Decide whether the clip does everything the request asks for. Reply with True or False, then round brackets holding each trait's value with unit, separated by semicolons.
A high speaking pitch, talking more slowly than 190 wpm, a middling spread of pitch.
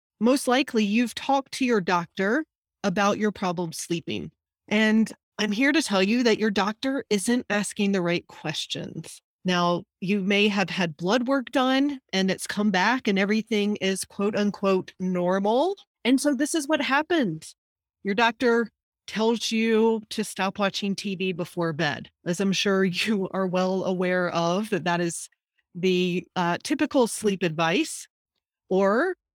True (205 Hz; 155 wpm; 4.2 semitones)